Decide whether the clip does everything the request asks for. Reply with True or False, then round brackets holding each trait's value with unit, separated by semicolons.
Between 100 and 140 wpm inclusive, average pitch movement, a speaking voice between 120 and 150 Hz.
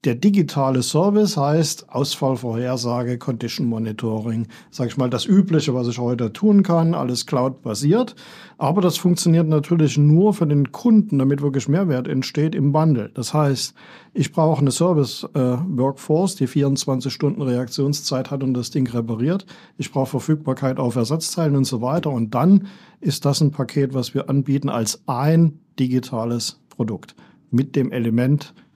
False (155 wpm; 4.1 semitones; 140 Hz)